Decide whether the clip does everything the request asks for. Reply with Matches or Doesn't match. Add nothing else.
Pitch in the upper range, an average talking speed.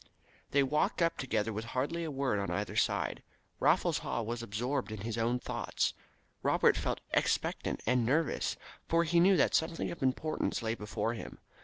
Doesn't match